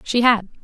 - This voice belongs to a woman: Yes, female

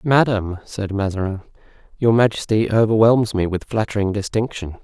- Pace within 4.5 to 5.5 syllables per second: Yes, 5.3 syllables/s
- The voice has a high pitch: No, low, 105 Hz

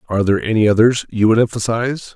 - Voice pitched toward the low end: Yes, low, 110 Hz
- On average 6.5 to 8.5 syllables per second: Yes, 7.0 syllables/s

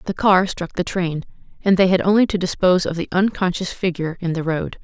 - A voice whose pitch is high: No, medium, 180 Hz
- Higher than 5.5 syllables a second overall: Yes, 5.9 syllables/s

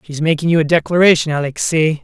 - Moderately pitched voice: Yes, medium, 160 Hz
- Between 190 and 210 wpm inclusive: Yes, fast, 205 wpm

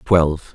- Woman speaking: No, male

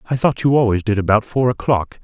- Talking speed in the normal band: No, fast, 235 wpm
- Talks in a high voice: No, low, 115 Hz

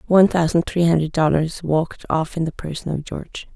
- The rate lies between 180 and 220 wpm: Yes, average, 200 wpm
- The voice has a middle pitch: Yes, medium, 165 Hz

